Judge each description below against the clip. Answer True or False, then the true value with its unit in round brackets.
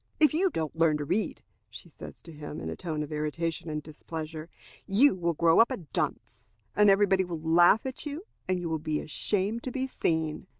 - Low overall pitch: False (170 Hz)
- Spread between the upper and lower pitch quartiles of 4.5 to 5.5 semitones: True (4.8 semitones)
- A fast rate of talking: True (215 wpm)